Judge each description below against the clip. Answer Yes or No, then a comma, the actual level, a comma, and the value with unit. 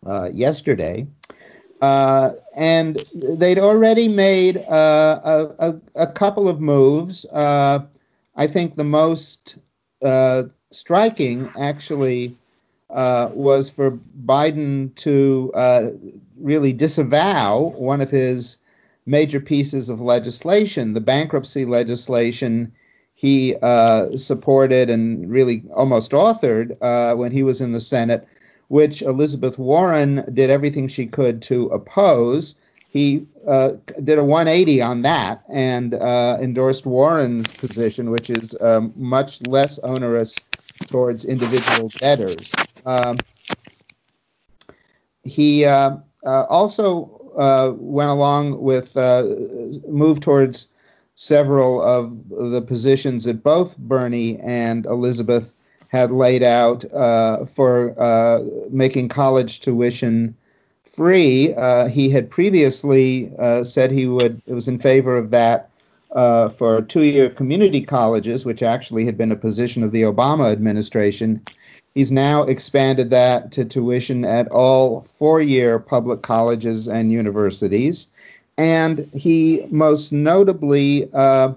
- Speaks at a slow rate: Yes, slow, 120 wpm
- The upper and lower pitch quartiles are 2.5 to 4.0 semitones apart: Yes, average, 3.1 semitones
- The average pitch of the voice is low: Yes, low, 130 Hz